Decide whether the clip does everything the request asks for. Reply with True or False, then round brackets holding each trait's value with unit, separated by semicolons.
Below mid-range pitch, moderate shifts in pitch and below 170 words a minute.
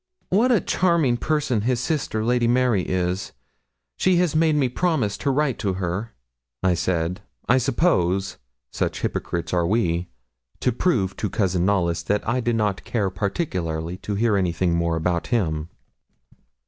False (105 Hz; 6.1 semitones; 155 wpm)